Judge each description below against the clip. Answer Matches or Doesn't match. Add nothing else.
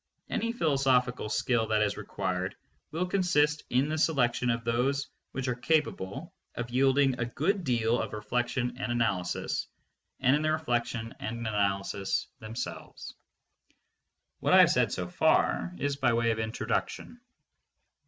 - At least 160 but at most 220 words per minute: Doesn't match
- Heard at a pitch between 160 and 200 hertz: Doesn't match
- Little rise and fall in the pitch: Doesn't match